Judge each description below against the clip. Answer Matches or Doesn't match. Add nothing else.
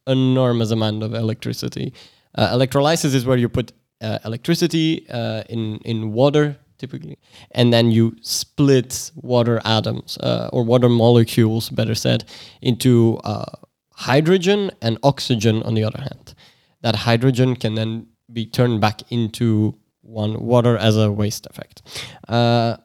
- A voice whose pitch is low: Matches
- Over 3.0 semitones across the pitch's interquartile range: Doesn't match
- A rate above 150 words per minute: Doesn't match